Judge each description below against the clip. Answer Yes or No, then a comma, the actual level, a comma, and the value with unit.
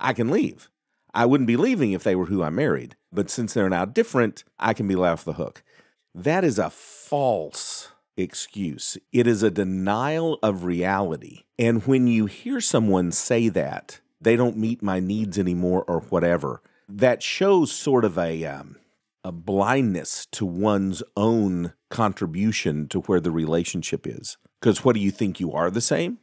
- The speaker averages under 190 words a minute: Yes, average, 175 wpm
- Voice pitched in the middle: No, low, 100 Hz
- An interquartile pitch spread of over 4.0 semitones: Yes, average, 4.5 semitones